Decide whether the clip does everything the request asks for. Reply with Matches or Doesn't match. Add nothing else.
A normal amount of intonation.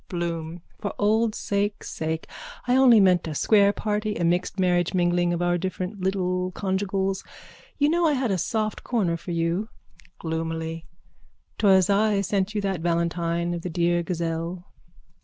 Matches